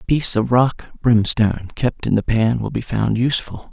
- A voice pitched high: No, low, 115 Hz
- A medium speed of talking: No, fast, 210 wpm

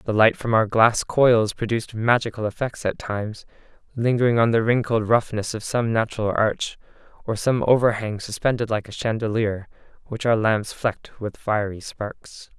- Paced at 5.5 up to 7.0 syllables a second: No, 4.9 syllables/s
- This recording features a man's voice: Yes, male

